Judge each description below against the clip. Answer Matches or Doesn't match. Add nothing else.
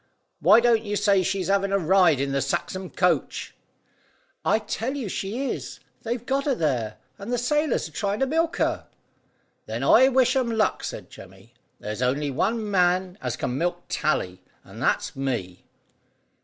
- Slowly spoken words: Doesn't match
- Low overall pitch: Doesn't match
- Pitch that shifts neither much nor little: Doesn't match